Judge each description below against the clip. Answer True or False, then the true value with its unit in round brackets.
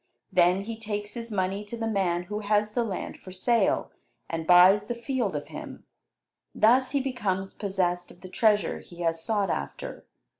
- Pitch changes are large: False (3.7 semitones)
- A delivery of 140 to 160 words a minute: False (180 wpm)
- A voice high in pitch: True (205 Hz)